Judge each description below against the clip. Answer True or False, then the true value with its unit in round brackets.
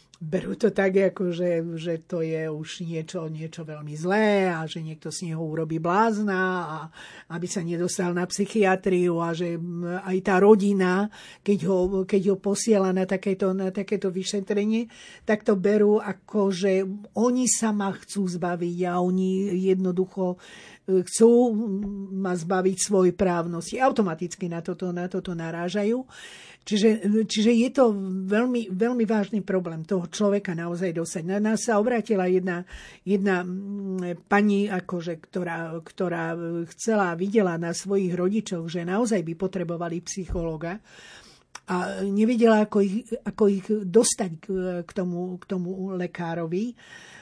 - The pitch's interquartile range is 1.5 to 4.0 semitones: True (2.8 semitones)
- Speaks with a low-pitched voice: False (190 Hz)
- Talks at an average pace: True (135 wpm)